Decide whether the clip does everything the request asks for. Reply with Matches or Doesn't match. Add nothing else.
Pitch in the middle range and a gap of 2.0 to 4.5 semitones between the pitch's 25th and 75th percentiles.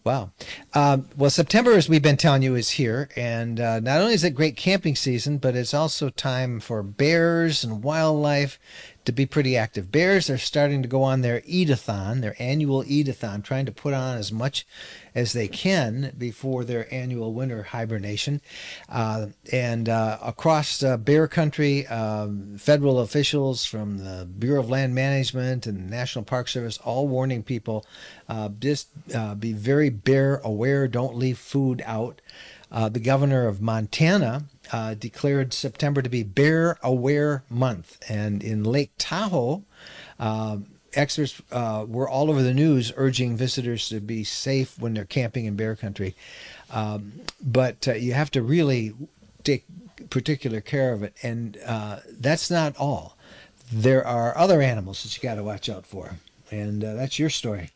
Doesn't match